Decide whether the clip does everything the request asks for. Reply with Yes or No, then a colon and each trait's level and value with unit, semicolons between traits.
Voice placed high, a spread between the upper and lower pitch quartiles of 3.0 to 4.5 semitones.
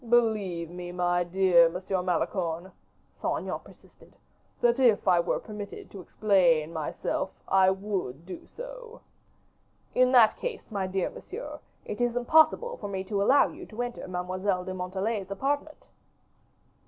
No: high, 195 Hz; average, 5.0 semitones